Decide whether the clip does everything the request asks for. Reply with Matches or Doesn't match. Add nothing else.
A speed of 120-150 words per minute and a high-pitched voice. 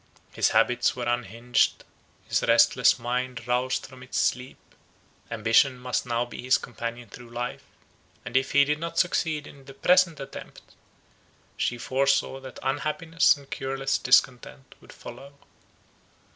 Doesn't match